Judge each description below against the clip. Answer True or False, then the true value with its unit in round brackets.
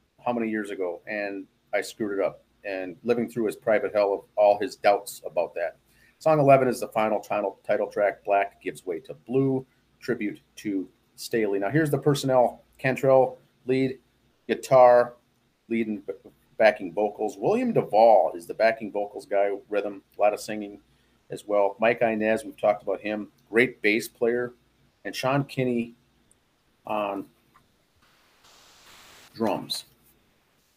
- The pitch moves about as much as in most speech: True (3.4 semitones)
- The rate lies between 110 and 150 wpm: True (145 wpm)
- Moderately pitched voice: False (115 Hz)